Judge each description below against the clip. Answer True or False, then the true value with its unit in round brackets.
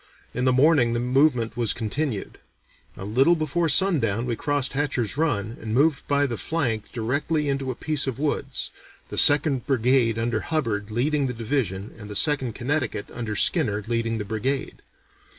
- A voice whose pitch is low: True (125 Hz)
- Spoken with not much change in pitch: False (4.2 semitones)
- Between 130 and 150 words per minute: False (170 wpm)